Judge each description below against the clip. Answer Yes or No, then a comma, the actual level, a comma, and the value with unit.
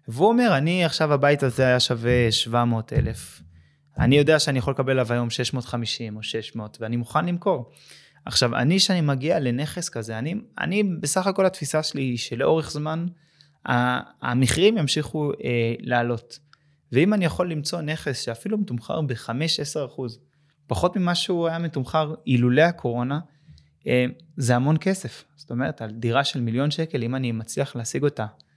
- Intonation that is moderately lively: Yes, average, 4.8 semitones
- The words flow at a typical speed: No, fast, 155 wpm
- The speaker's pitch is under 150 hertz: Yes, medium, 140 Hz